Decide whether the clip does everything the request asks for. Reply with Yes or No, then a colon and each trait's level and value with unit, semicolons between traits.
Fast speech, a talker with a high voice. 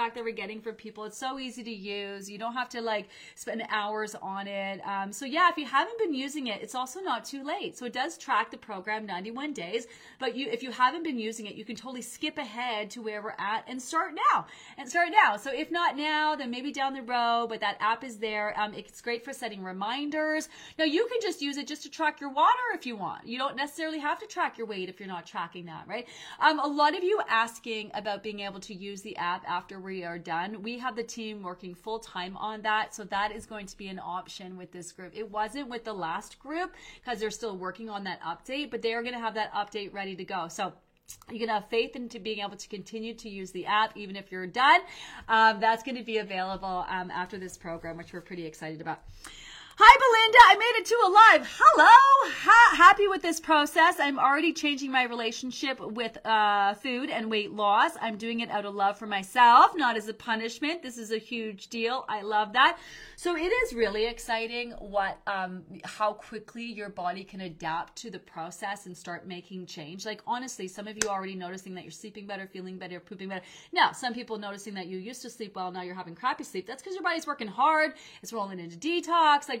Yes: fast, 235 wpm; high, 225 Hz